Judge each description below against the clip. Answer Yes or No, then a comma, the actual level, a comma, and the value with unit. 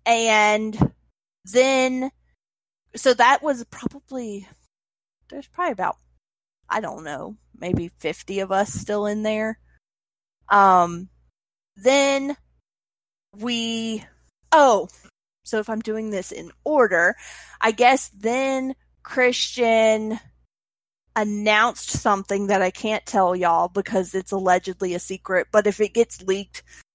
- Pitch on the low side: No, high, 215 Hz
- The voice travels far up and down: No, average, 3.8 semitones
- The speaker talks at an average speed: No, slow, 115 wpm